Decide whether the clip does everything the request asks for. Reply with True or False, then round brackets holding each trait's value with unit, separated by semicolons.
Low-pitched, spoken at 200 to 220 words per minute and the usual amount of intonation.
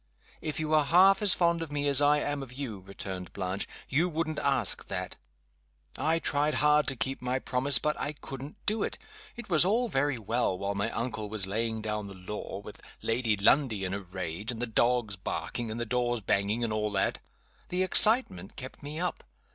False (125 Hz; 205 wpm; 6.2 semitones)